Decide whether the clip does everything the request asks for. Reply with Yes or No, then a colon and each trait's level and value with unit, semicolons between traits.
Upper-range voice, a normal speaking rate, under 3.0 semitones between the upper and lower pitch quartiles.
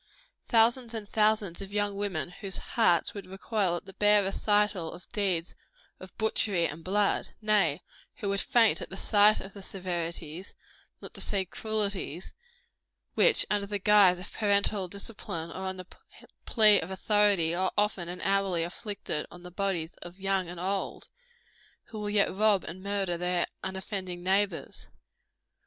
Yes: high, 195 Hz; average, 160 wpm; narrow, 2.5 semitones